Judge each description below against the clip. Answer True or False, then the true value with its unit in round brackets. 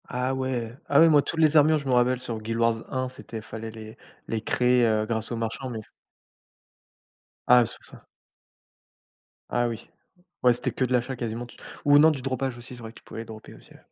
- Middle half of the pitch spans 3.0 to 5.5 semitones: False (2.5 semitones)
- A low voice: True (120 Hz)